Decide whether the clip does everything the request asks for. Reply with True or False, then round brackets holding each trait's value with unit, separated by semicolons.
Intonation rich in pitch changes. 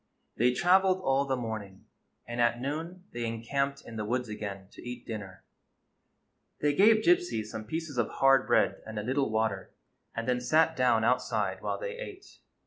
True (5.8 semitones)